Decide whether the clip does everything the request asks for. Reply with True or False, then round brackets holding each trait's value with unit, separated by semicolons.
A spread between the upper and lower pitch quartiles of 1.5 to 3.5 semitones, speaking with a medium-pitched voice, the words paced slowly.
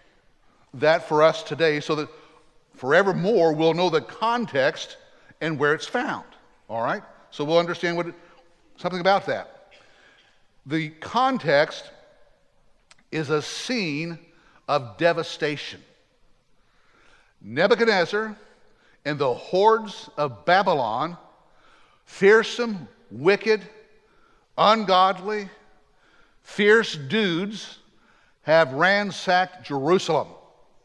False (5.5 semitones; 175 Hz; 90 wpm)